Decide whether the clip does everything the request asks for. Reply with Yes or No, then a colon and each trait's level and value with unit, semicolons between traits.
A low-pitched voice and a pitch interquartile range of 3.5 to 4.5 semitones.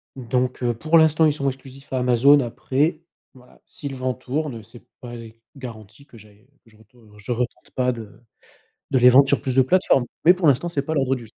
No: low, 130 Hz; average, 2.8 semitones